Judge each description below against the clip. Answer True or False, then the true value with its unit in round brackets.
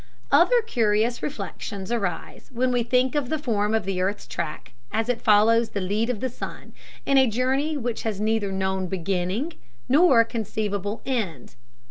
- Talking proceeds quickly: False (165 wpm)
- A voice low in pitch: False (225 Hz)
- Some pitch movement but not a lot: True (3.9 semitones)